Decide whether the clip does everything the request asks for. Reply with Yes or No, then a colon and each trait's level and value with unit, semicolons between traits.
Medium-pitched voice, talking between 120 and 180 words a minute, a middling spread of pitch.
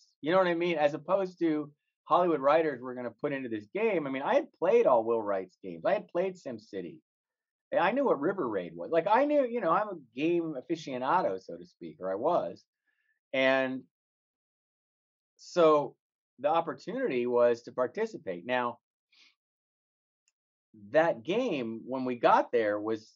No: medium, 145 Hz; average, 170 wpm; wide, 6.7 semitones